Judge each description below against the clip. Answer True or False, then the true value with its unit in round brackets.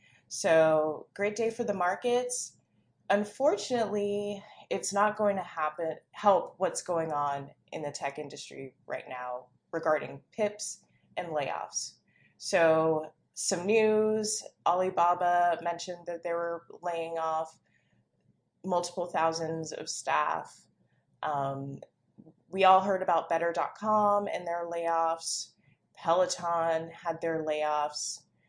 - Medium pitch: True (170 Hz)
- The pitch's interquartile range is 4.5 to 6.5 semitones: False (3.7 semitones)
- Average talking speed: False (110 wpm)